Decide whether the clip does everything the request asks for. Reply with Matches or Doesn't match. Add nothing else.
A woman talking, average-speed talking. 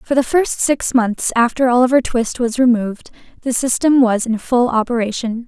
Matches